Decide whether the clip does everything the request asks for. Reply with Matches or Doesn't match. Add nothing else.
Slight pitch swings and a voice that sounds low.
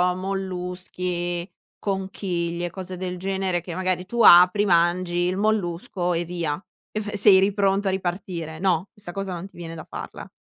Doesn't match